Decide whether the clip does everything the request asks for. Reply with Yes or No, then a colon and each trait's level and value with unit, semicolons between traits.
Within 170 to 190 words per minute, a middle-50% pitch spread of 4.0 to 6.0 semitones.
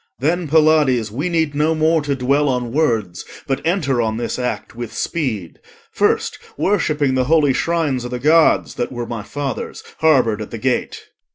Yes: average, 175 wpm; average, 4.5 semitones